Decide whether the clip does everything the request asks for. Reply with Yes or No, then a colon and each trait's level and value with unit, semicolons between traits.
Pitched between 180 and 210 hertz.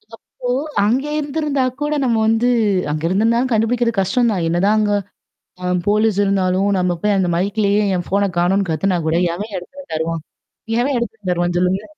Yes: high, 205 Hz